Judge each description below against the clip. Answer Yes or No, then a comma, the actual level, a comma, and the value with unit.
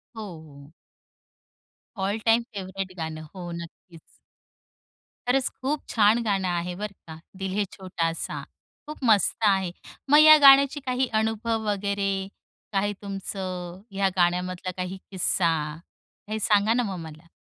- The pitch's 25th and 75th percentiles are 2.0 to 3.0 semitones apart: No, average, 3.6 semitones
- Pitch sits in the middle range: No, high, 195 Hz